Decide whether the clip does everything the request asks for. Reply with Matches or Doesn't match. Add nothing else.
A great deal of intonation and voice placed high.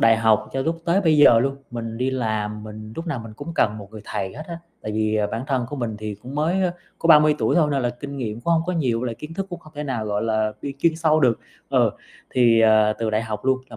Doesn't match